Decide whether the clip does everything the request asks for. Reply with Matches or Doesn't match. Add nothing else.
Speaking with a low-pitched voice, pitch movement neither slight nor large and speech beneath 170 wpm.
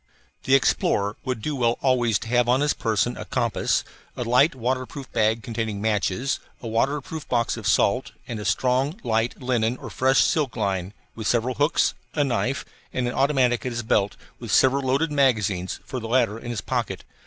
Doesn't match